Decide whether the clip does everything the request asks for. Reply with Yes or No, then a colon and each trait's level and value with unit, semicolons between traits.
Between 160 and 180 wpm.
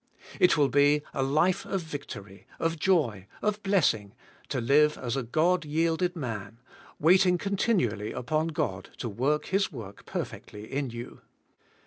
No: average, 145 wpm